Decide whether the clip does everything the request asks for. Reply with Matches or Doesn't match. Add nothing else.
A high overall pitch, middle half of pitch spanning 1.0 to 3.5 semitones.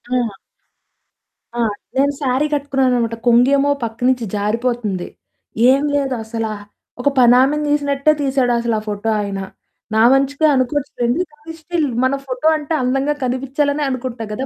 Matches